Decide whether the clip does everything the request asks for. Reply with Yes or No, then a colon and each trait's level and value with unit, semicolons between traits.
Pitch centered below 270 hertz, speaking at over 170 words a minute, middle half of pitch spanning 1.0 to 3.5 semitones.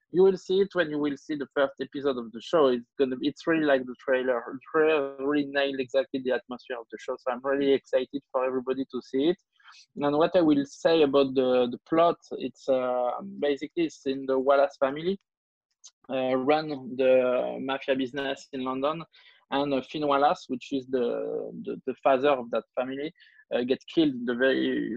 Yes: medium, 140 Hz; average, 190 wpm; average, 2.9 semitones